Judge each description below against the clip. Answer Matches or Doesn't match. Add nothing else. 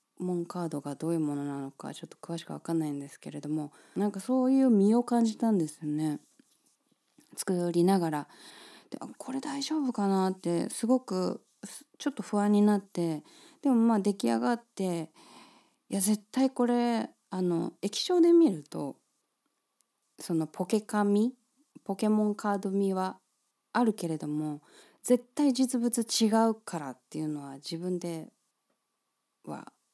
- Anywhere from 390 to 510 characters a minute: Doesn't match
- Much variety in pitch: Matches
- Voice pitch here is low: Doesn't match